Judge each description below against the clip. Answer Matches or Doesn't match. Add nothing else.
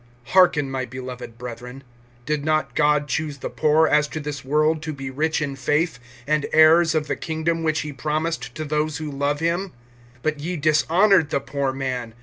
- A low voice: Doesn't match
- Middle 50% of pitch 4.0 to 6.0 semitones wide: Doesn't match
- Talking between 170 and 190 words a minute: Matches